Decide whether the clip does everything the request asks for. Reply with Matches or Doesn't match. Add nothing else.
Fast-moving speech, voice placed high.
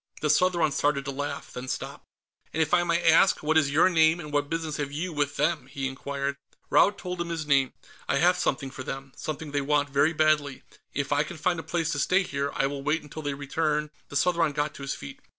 Doesn't match